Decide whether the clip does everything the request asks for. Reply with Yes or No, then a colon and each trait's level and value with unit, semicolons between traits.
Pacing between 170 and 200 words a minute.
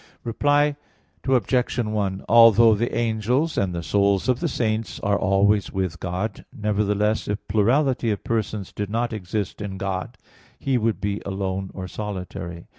No: average, 150 wpm